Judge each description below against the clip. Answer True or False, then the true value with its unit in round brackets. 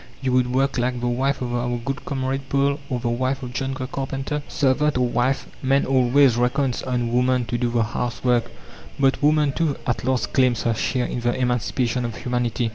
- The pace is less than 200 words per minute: False (205 wpm)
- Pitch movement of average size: False (1.8 semitones)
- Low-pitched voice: True (125 Hz)